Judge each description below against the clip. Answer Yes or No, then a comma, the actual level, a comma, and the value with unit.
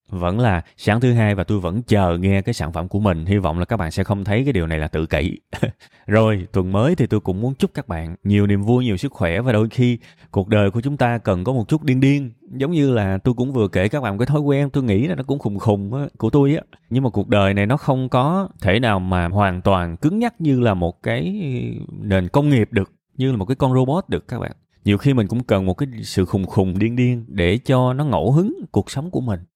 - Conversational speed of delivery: No, fast, 275 wpm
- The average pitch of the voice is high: No, low, 110 Hz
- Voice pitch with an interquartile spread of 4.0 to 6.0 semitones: Yes, average, 5.2 semitones